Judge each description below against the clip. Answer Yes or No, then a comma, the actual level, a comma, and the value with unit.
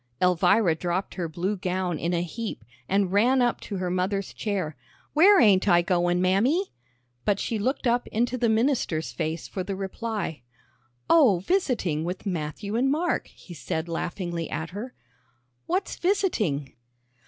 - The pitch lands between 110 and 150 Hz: No, high, 195 Hz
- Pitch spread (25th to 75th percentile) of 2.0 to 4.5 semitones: No, average, 5.2 semitones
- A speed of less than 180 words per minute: Yes, average, 155 wpm